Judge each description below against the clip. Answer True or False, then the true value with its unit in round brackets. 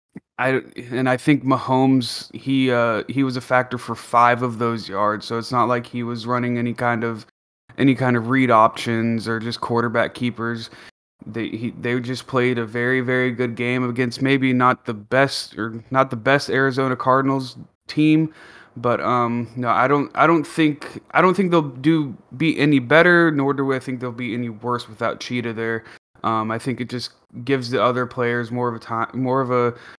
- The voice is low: True (125 Hz)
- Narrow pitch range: True (2.1 semitones)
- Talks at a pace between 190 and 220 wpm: True (200 wpm)